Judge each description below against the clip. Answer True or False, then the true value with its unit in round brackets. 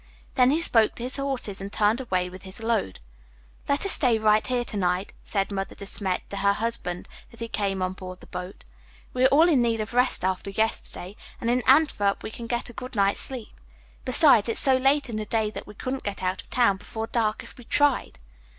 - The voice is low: False (225 Hz)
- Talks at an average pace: False (230 wpm)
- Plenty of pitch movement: False (4.1 semitones)